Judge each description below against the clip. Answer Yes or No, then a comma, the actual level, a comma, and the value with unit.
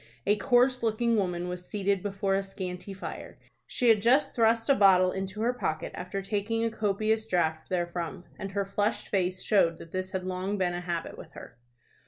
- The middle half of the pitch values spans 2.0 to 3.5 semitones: Yes, average, 3.2 semitones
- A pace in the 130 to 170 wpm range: No, average, 195 wpm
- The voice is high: Yes, high, 195 Hz